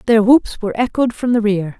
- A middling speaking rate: No, fast, 235 wpm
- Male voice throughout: No, female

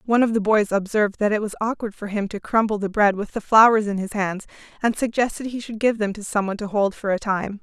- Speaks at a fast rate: Yes, fast, 275 wpm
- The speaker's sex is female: Yes, female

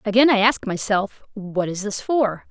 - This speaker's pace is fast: No, average, 190 wpm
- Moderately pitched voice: No, high, 215 Hz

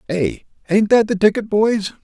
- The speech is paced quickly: No, average, 175 wpm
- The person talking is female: No, male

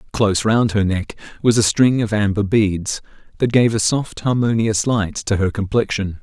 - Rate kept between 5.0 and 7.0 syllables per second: No, 4.7 syllables/s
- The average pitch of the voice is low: Yes, low, 105 Hz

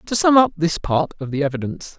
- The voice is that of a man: Yes, male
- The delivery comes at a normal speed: No, fast, 240 wpm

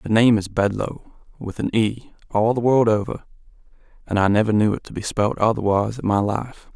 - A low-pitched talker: Yes, low, 110 Hz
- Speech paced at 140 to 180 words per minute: No, fast, 205 wpm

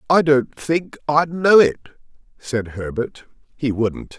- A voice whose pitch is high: No, medium, 140 Hz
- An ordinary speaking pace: Yes, average, 145 wpm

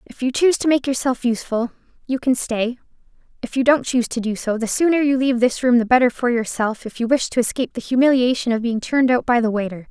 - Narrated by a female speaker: Yes, female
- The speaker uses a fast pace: Yes, fast, 250 wpm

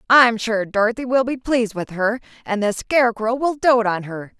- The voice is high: Yes, high, 225 Hz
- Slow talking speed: No, fast, 205 wpm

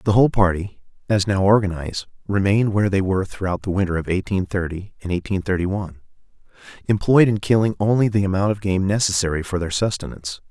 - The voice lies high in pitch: No, very low, 95 Hz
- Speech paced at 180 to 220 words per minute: Yes, average, 185 wpm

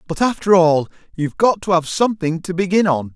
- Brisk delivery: Yes, fast, 210 wpm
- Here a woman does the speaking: No, male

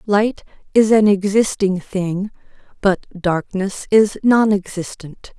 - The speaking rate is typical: No, slow, 100 wpm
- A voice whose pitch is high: Yes, high, 200 Hz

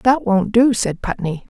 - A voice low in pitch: No, high, 215 Hz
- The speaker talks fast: No, average, 190 wpm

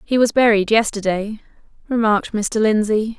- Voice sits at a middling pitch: No, high, 215 Hz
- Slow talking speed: Yes, slow, 130 wpm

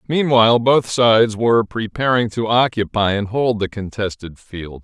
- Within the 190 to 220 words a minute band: No, average, 150 wpm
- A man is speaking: Yes, male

